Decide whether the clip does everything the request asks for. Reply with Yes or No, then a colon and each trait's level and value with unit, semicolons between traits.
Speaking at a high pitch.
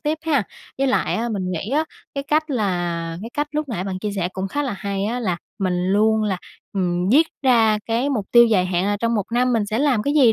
Yes: high, 220 Hz